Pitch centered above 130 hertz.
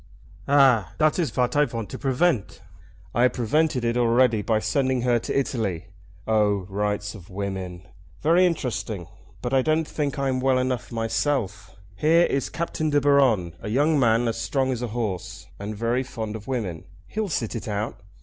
No: low, 120 Hz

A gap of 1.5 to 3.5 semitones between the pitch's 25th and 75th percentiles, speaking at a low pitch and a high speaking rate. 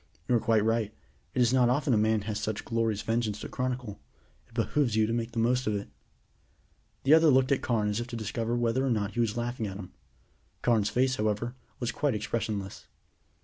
Yes: narrow, 2.5 semitones; low, 115 Hz; fast, 210 wpm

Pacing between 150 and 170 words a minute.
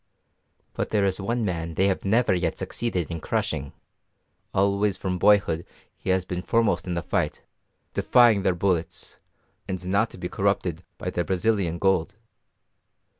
Yes: average, 155 wpm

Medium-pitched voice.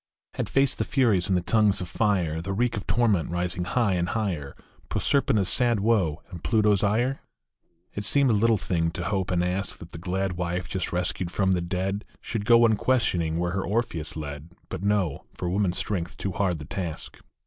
No: very low, 95 Hz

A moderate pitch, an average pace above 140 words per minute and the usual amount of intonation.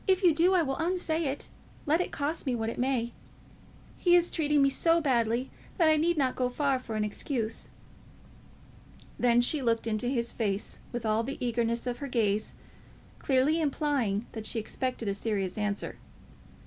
No: very high, 255 Hz; average, 180 wpm; average, 4.9 semitones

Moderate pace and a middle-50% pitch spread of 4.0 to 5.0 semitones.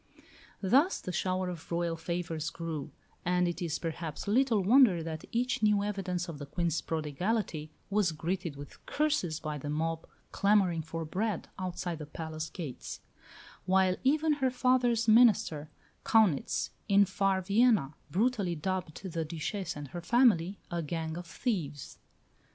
Yes: average, 145 wpm; average, 4.5 semitones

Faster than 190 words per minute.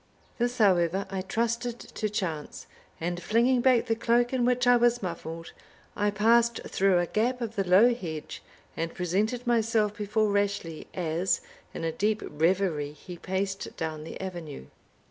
No: average, 160 wpm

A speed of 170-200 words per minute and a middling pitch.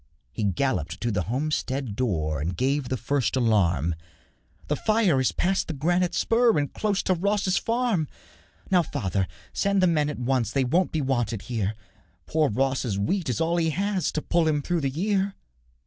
Yes: average, 180 wpm; medium, 145 Hz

